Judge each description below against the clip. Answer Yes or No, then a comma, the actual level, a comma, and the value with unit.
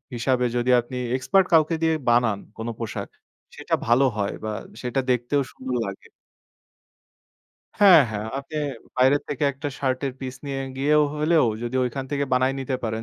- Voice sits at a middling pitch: No, low, 130 Hz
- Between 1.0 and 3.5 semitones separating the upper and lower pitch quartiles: Yes, average, 3.0 semitones